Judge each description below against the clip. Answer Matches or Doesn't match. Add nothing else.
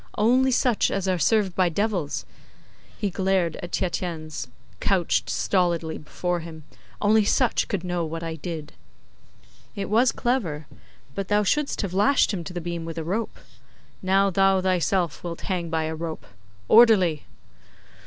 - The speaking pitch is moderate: Matches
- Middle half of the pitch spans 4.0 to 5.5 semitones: Doesn't match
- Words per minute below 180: Matches